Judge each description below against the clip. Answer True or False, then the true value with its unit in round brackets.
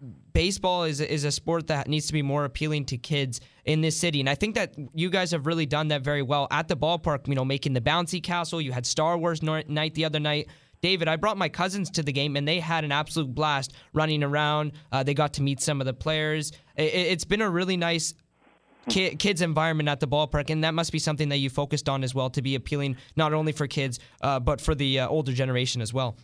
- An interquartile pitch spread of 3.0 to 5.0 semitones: False (2.4 semitones)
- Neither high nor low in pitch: True (150 Hz)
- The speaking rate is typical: False (250 wpm)